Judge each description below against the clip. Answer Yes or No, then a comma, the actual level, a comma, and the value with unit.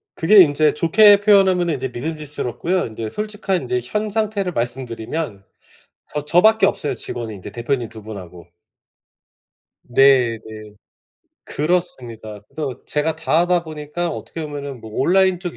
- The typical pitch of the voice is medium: Yes, medium, 150 Hz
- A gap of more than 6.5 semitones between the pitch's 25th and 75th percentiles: Yes, wide, 7.1 semitones